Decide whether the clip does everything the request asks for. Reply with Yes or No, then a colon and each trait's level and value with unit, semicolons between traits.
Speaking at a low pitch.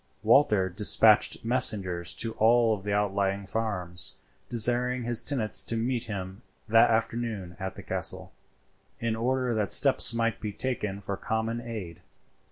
Yes: low, 110 Hz